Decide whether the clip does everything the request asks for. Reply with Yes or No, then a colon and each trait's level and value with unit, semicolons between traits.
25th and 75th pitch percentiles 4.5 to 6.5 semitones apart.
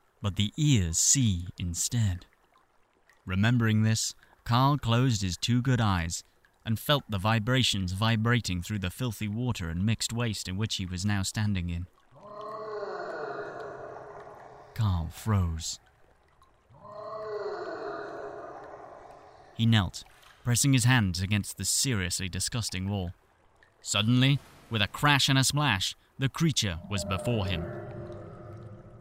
Yes: average, 4.9 semitones